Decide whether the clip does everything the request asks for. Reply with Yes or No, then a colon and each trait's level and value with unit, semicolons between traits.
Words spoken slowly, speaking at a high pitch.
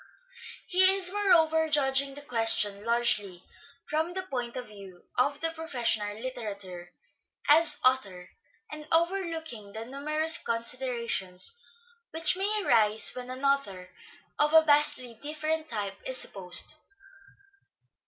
Yes: slow, 120 wpm; very high, 260 Hz